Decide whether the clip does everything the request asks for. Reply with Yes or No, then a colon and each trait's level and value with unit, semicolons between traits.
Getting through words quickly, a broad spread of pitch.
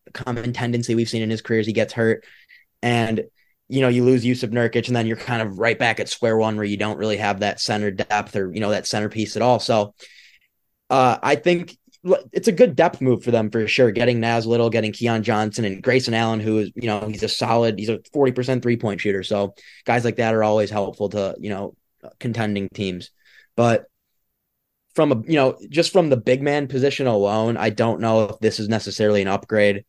No: fast, 225 wpm; narrow, 2.6 semitones